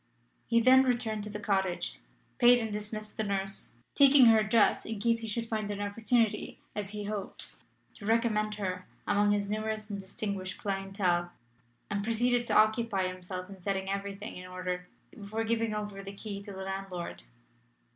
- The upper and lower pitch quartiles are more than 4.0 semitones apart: No, narrow, 2.4 semitones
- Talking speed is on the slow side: No, average, 170 wpm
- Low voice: No, high, 205 Hz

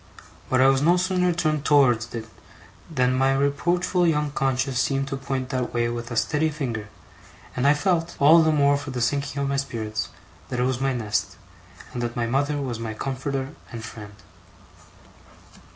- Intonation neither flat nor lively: Yes, average, 3.3 semitones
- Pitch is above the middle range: No, low, 135 Hz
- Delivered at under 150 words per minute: No, average, 185 wpm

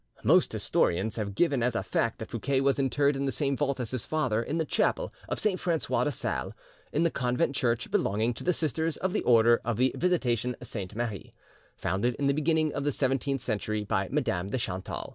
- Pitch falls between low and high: No, low, 130 Hz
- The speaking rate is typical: No, fast, 215 wpm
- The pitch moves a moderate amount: Yes, average, 4.2 semitones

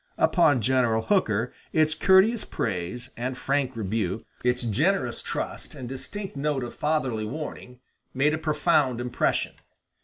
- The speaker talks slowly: Yes, slow, 130 wpm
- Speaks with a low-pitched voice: Yes, low, 130 Hz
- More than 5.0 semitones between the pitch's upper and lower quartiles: No, average, 4.5 semitones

